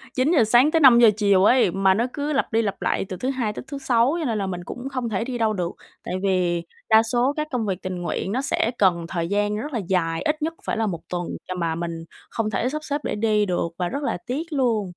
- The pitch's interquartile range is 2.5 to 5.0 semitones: No, wide, 5.6 semitones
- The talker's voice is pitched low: No, high, 220 Hz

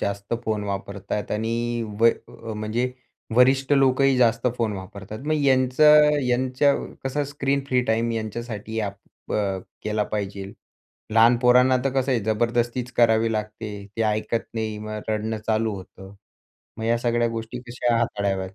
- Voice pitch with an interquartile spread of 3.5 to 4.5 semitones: No, average, 2.8 semitones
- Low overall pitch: Yes, low, 115 Hz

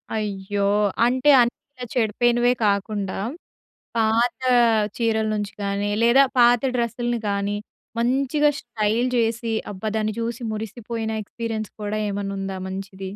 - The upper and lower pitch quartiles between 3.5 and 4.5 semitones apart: No, average, 2.9 semitones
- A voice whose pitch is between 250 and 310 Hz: No, high, 220 Hz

